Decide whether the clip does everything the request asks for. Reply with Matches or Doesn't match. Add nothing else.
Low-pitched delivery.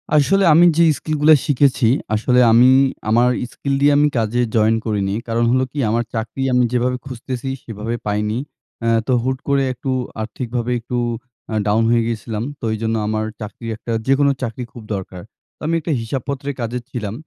Matches